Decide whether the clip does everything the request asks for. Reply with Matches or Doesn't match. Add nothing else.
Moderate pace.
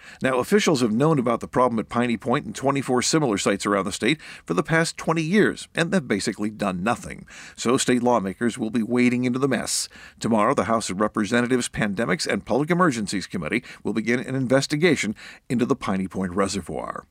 Matches